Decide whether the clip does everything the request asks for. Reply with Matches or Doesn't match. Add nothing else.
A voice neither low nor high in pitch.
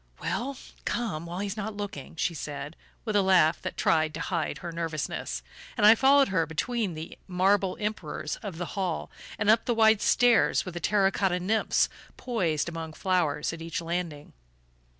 Matches